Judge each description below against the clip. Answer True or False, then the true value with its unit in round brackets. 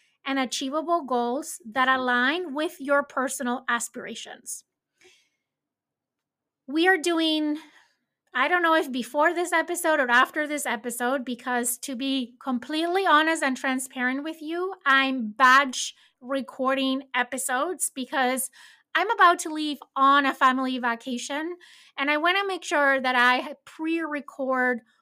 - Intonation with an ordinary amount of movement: True (3.8 semitones)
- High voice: True (275 Hz)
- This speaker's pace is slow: True (130 wpm)